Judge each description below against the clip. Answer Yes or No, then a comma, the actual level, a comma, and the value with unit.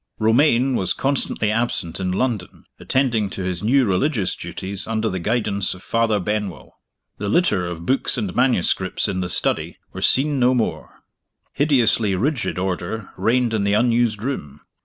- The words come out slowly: No, average, 160 wpm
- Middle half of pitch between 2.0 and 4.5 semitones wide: No, average, 5.0 semitones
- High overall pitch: No, low, 110 Hz